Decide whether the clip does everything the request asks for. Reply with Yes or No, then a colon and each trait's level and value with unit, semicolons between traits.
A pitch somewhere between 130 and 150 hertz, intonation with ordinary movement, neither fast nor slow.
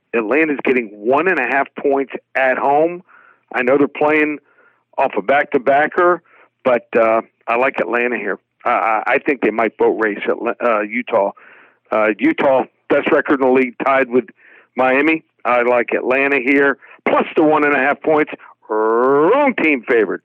Yes: medium, 140 Hz; average, 3.3 semitones; average, 180 wpm